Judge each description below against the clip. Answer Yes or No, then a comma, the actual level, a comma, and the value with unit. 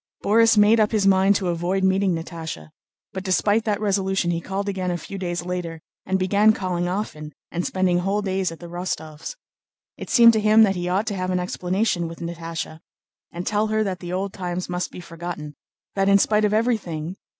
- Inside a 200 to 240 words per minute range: Yes, fast, 205 wpm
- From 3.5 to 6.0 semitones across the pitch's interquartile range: No, average, 2.7 semitones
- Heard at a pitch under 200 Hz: Yes, medium, 185 Hz